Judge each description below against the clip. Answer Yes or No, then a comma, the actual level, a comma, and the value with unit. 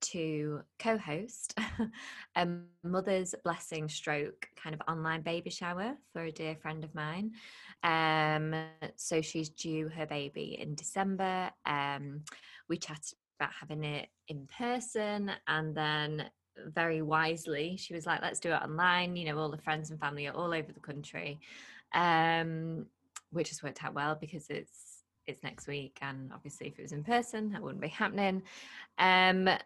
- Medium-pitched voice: Yes, medium, 160 Hz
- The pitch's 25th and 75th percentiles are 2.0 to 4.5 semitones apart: Yes, average, 3.1 semitones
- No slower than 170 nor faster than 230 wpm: No, average, 160 wpm